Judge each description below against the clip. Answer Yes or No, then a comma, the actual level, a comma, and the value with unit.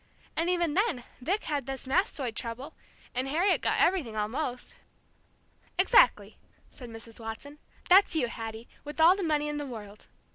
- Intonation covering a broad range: Yes, wide, 6.5 semitones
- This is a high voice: Yes, very high, 285 Hz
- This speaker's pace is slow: No, average, 155 wpm